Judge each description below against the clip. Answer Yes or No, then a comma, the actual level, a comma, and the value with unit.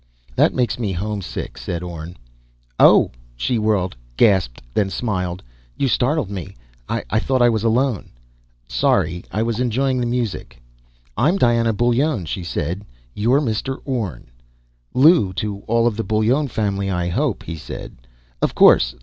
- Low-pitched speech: Yes, low, 110 Hz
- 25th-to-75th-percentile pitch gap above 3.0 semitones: Yes, average, 4.9 semitones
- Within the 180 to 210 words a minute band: No, average, 150 wpm